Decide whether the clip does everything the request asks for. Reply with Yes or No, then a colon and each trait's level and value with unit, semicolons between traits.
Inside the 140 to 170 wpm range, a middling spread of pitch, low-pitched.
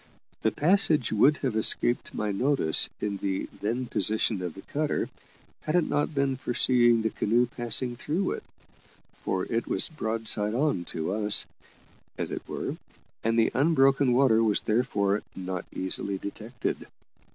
Yes: average, 150 wpm; average, 4.5 semitones; low, 115 Hz